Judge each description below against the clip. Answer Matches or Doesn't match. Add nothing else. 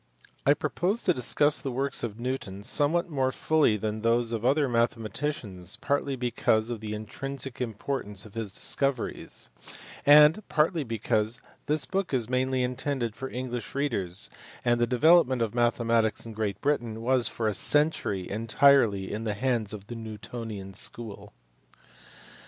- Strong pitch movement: Doesn't match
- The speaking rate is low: Doesn't match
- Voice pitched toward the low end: Matches